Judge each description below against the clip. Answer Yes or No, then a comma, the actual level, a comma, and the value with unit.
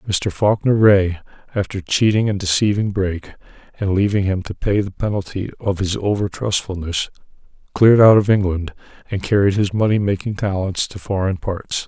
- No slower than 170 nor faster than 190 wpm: No, average, 160 wpm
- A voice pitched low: Yes, low, 100 Hz